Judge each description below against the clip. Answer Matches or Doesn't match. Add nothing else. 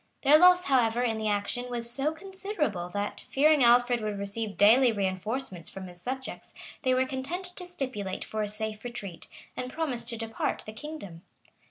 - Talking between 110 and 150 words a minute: Doesn't match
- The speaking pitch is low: Doesn't match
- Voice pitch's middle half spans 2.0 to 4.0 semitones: Doesn't match